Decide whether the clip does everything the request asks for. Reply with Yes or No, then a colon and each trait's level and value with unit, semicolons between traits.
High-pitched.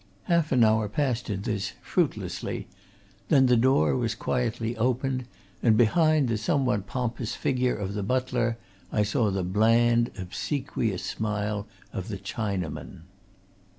No: low, 115 Hz